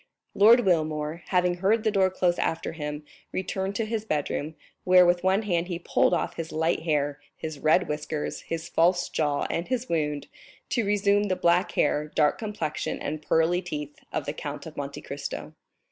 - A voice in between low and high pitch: Yes, medium, 175 Hz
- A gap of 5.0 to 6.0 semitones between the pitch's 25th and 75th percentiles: No, average, 3.8 semitones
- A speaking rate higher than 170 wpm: Yes, average, 180 wpm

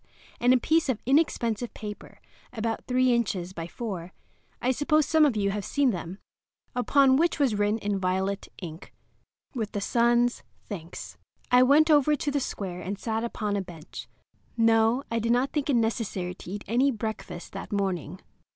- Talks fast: No, average, 170 wpm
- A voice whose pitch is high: Yes, high, 225 Hz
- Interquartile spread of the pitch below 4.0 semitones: No, average, 4.6 semitones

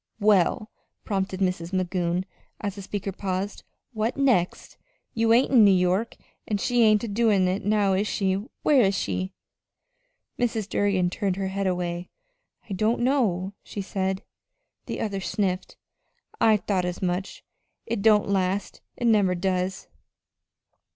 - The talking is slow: No, average, 145 wpm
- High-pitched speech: Yes, high, 195 Hz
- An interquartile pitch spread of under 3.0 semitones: Yes, narrow, 2.5 semitones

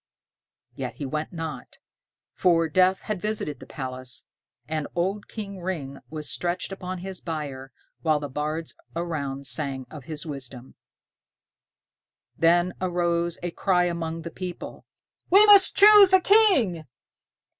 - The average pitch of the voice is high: No, medium, 170 Hz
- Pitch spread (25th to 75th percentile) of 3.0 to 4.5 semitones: Yes, average, 3.8 semitones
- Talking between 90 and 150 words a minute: Yes, slow, 135 wpm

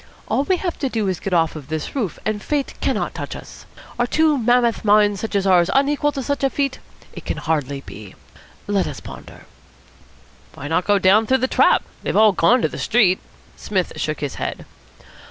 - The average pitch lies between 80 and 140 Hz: No, high, 210 Hz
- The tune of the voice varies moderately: No, wide, 6.7 semitones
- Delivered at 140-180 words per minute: No, fast, 205 wpm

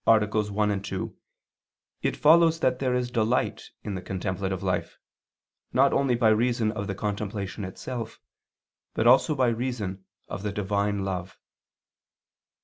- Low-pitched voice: Yes, low, 105 Hz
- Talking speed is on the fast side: No, average, 140 wpm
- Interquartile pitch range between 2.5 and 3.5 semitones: No, average, 3.9 semitones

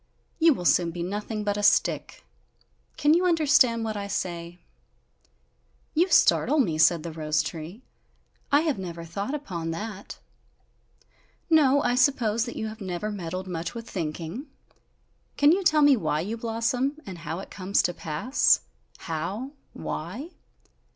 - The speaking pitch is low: No, high, 205 Hz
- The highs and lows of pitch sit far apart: Yes, wide, 7.5 semitones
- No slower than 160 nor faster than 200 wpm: No, average, 150 wpm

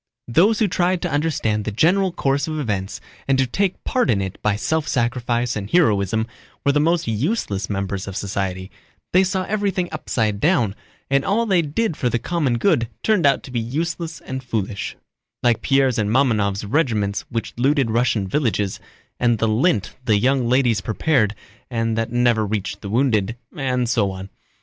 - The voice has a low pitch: Yes, low, 120 Hz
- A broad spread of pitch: Yes, wide, 6.6 semitones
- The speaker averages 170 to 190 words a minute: Yes, average, 175 wpm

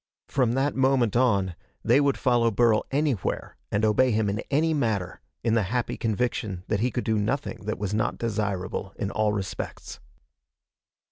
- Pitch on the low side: Yes, low, 110 Hz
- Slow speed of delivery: No, average, 165 wpm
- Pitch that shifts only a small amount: No, average, 3.5 semitones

